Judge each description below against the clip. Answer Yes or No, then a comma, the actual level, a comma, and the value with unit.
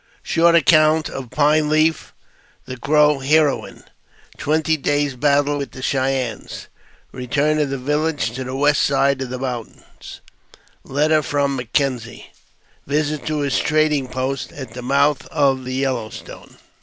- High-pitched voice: No, medium, 140 Hz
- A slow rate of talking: No, average, 155 wpm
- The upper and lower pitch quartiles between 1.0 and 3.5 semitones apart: Yes, narrow, 2.5 semitones